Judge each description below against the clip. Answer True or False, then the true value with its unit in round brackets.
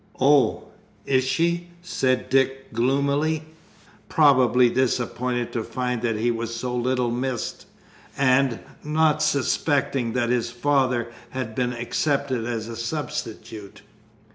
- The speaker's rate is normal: False (115 wpm)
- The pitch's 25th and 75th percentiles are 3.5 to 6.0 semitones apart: False (2.9 semitones)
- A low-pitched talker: True (130 Hz)